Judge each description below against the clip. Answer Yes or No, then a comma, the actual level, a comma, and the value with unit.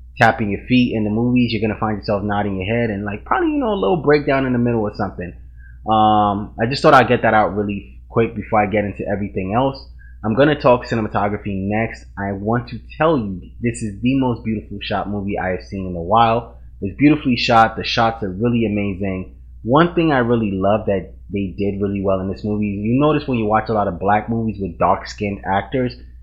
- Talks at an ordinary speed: No, fast, 230 wpm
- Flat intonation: No, average, 3.1 semitones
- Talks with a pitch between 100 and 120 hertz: Yes, low, 105 Hz